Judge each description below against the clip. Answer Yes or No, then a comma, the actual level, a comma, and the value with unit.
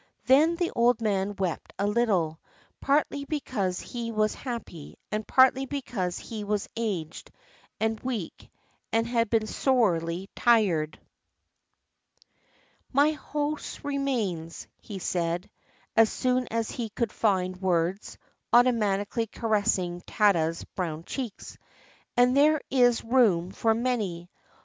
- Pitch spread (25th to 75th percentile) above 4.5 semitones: Yes, average, 5.1 semitones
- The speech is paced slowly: Yes, slow, 115 wpm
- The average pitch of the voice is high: Yes, high, 220 Hz